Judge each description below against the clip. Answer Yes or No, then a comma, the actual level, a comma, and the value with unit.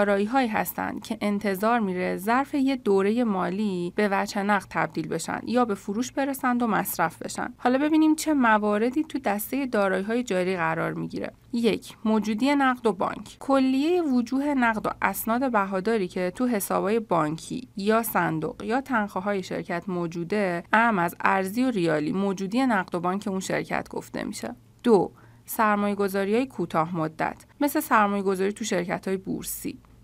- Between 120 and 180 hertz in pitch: No, high, 210 Hz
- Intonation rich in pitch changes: No, average, 4.5 semitones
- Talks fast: Yes, fast, 160 wpm